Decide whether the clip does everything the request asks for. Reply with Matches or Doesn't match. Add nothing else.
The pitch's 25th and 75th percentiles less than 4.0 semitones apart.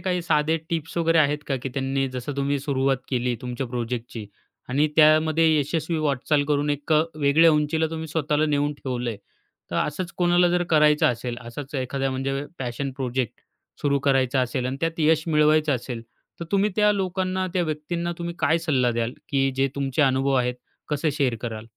Matches